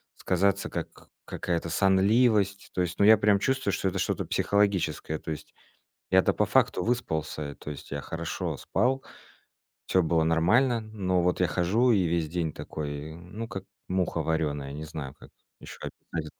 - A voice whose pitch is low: Yes, very low, 90 Hz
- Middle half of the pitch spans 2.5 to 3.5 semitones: No, average, 4.3 semitones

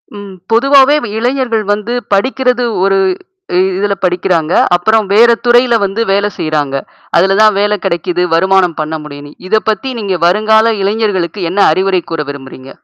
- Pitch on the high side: Yes, high, 200 Hz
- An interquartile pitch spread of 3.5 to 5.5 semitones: Yes, average, 4.0 semitones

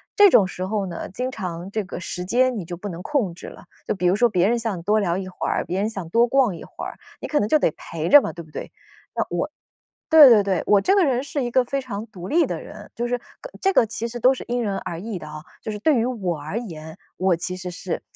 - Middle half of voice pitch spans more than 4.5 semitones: Yes, average, 5.2 semitones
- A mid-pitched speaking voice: No, high, 210 Hz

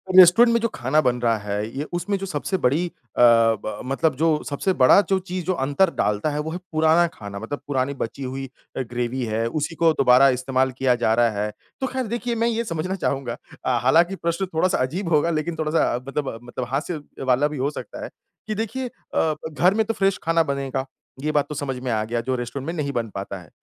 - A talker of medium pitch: Yes, medium, 145 Hz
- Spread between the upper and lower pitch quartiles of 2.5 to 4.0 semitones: No, wide, 5.6 semitones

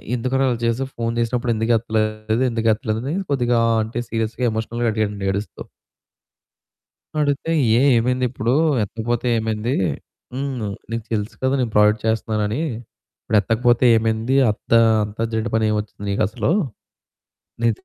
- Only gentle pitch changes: Yes, narrow, 1.9 semitones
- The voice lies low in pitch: Yes, low, 115 Hz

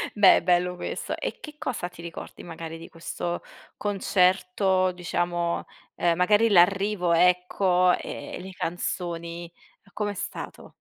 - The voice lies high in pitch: No, medium, 180 Hz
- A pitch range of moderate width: No, narrow, 1.8 semitones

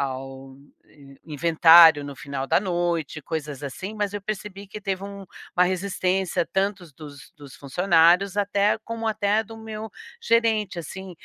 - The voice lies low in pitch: No, medium, 185 Hz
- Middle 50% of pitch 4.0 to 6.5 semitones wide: Yes, average, 5.0 semitones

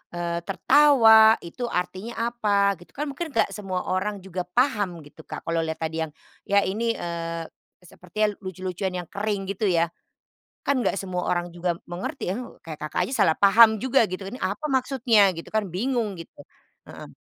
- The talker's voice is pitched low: No, high, 195 Hz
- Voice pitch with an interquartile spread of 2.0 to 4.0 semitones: No, average, 4.4 semitones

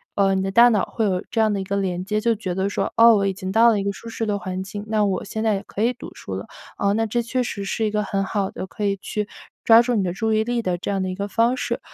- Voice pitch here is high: Yes, high, 205 Hz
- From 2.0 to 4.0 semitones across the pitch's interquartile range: Yes, narrow, 2.5 semitones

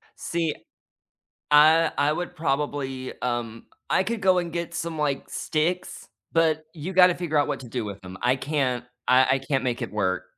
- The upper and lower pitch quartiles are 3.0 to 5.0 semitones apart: Yes, average, 4.6 semitones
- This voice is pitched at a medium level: Yes, medium, 150 Hz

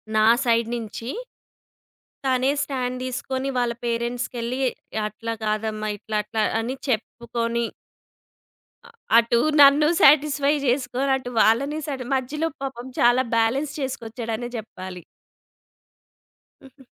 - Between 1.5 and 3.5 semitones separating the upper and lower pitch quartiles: Yes, average, 2.7 semitones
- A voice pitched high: Yes, high, 245 Hz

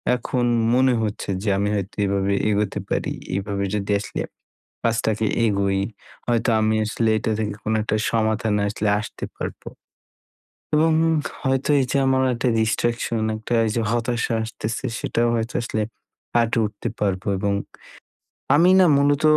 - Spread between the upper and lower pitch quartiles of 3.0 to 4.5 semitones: No, narrow, 2.4 semitones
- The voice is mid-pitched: No, low, 110 Hz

